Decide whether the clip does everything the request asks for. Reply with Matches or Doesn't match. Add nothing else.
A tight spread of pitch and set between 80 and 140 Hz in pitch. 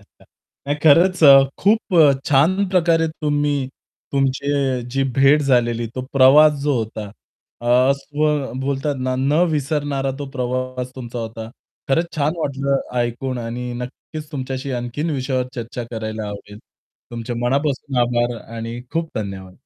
Doesn't match